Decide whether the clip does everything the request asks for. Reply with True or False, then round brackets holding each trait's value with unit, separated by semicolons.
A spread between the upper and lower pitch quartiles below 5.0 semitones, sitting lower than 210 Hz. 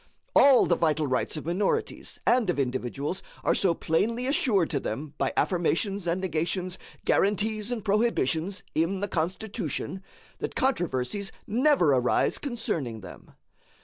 False (5.3 semitones; 185 Hz)